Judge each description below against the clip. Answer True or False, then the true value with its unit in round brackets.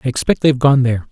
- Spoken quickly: True (270 wpm)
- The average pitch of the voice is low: True (130 Hz)